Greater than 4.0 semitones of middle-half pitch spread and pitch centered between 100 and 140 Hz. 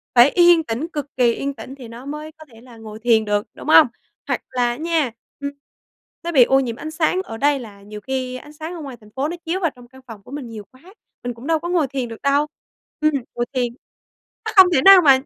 No: average, 4.5 semitones; very high, 265 Hz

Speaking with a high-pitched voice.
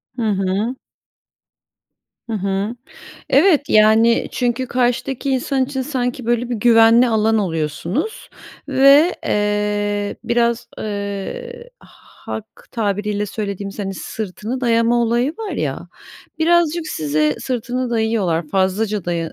Yes: high, 225 Hz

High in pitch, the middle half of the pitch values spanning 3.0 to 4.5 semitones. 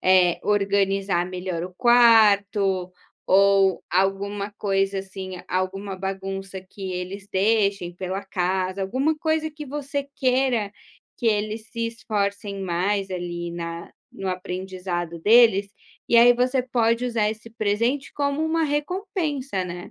Yes: high, 200 Hz; average, 3.8 semitones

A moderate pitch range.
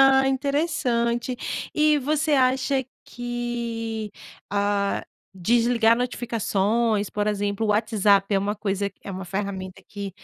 Yes: average, 3.6 semitones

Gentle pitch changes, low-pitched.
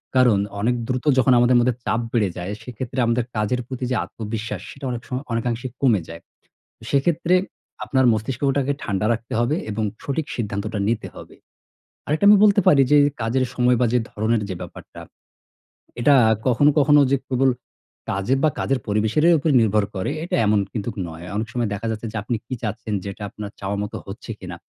No: average, 3.7 semitones; low, 120 Hz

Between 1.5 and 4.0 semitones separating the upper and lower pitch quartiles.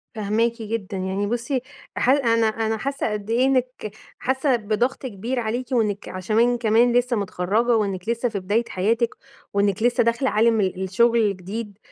Yes: average, 2.8 semitones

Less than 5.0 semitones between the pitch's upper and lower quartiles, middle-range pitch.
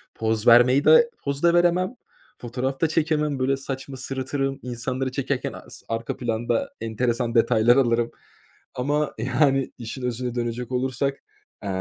No: average, 2.8 semitones; low, 130 Hz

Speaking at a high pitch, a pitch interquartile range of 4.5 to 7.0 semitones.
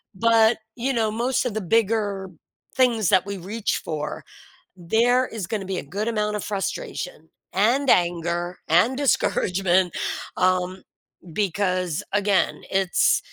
No: high, 200 Hz; average, 3.9 semitones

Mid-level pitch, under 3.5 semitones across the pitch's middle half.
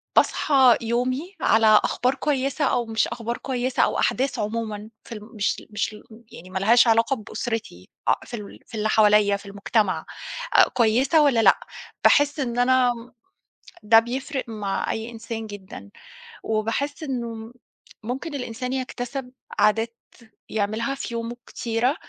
No: high, 230 Hz; average, 3.0 semitones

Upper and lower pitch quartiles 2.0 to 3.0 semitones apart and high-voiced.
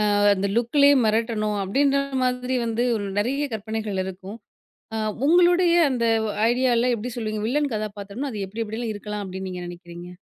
No: average, 3.7 semitones; high, 220 Hz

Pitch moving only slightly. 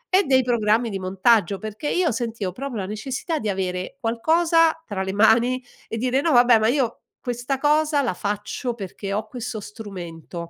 No: average, 4.4 semitones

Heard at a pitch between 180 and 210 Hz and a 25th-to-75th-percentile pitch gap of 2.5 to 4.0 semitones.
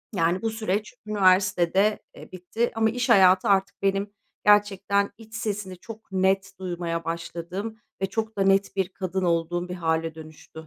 Yes: high, 190 Hz; average, 2.8 semitones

